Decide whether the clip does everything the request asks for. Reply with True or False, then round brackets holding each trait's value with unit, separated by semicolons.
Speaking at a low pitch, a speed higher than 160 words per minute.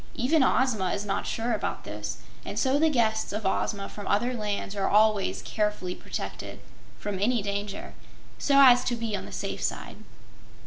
False (215 Hz; 175 wpm)